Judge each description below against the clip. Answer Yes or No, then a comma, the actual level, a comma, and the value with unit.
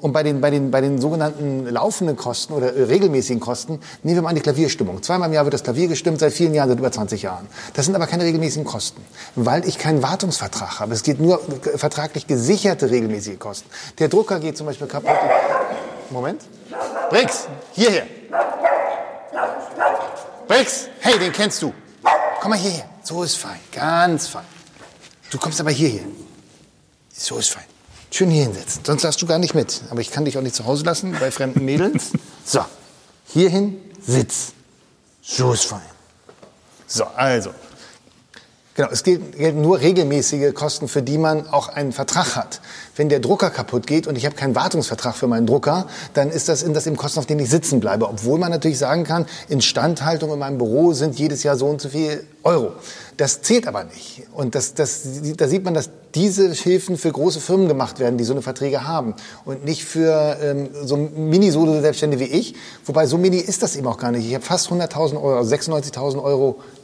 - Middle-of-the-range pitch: Yes, medium, 150 Hz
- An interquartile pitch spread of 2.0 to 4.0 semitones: Yes, average, 3.6 semitones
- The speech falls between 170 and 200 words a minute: Yes, fast, 190 wpm